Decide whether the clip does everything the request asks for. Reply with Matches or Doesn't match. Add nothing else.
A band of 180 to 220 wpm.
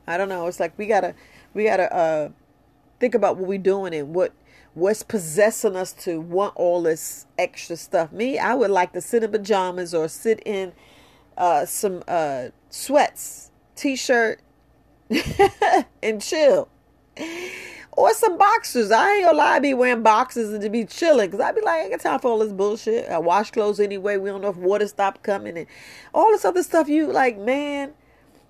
Matches